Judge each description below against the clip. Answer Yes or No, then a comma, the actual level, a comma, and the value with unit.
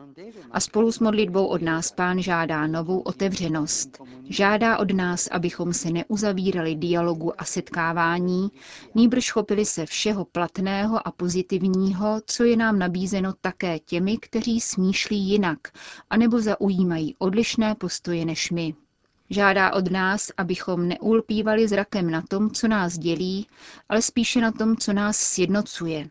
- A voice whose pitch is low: No, high, 190 Hz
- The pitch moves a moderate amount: Yes, average, 3.7 semitones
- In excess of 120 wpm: Yes, average, 135 wpm